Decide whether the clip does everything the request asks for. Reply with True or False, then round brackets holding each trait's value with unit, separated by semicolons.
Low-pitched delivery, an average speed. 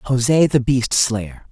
True (125 Hz; 160 wpm)